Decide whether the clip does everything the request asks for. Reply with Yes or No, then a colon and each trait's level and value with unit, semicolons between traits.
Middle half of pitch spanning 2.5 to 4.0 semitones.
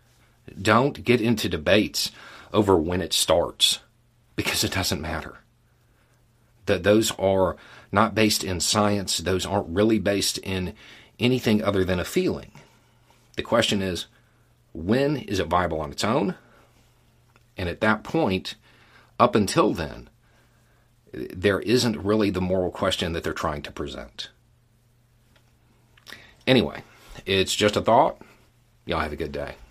Yes: average, 3.2 semitones